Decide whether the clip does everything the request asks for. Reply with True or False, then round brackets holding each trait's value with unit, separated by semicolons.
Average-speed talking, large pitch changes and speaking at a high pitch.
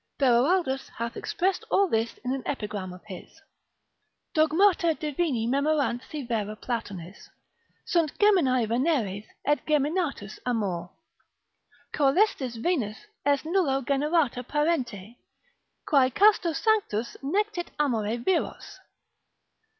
False (105 wpm; 6.2 semitones; 270 Hz)